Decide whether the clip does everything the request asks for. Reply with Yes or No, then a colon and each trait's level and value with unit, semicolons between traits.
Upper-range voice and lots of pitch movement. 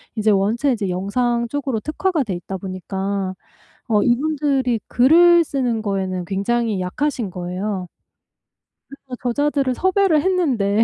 Yes: high, 235 Hz; wide, 6.4 semitones